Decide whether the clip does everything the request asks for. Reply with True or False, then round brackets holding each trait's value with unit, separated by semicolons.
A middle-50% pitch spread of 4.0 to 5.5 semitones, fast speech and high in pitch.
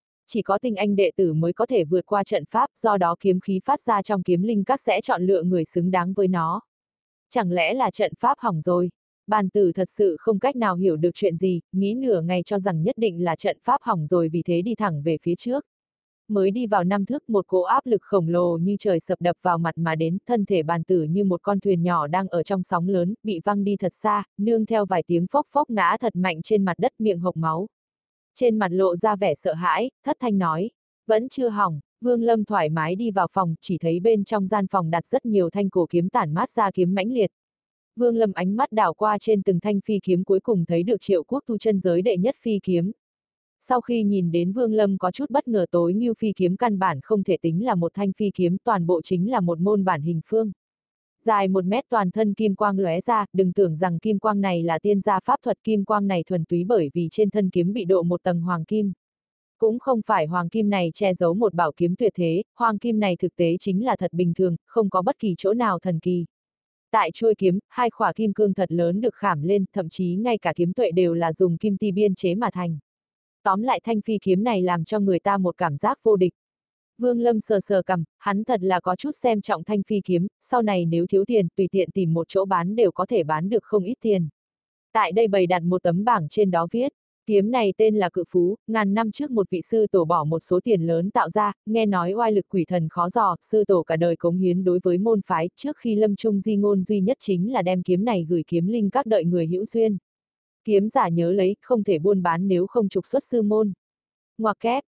False (3.5 semitones; 255 wpm; 195 Hz)